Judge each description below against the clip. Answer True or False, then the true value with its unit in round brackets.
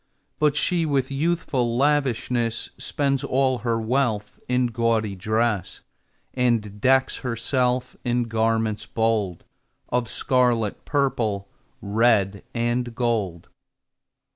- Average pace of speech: False (100 wpm)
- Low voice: True (120 Hz)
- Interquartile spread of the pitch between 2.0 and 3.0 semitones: True (2.7 semitones)